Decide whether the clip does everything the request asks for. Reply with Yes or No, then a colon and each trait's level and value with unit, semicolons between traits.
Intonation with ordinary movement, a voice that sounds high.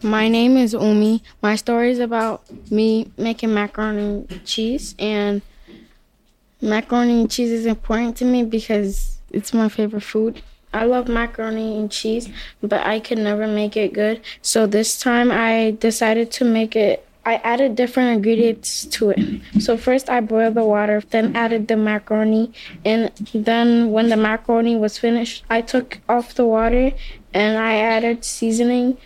No: narrow, 1.5 semitones; high, 225 Hz